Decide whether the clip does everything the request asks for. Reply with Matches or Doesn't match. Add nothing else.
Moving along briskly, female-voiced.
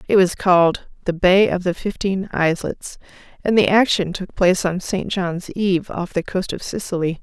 Doesn't match